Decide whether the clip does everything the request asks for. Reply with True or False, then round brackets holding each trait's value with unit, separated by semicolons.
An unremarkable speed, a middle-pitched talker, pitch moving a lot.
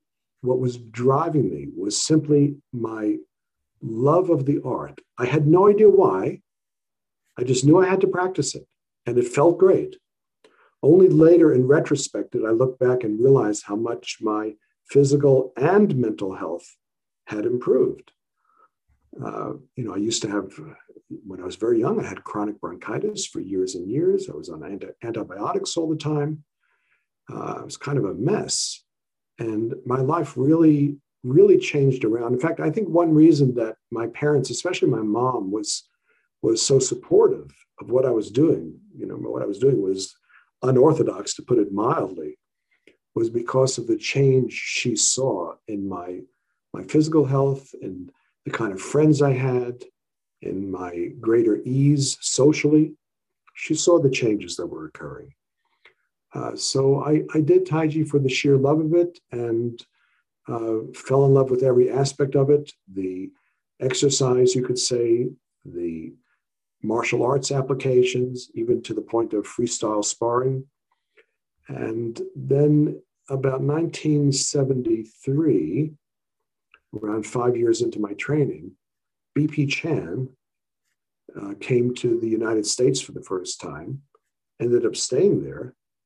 True (150 wpm; 145 Hz; 6.9 semitones)